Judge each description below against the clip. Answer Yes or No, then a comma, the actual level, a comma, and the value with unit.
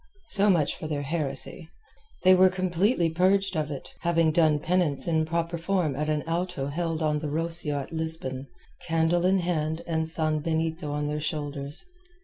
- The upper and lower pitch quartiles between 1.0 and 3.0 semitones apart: Yes, narrow, 2.4 semitones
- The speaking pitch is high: No, medium, 160 Hz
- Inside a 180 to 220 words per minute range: No, average, 165 wpm